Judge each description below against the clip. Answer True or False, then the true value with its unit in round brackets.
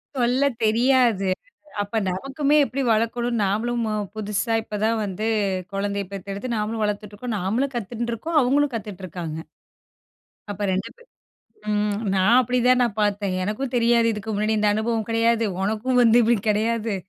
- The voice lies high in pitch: True (220 Hz)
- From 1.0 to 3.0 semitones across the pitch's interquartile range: True (2.7 semitones)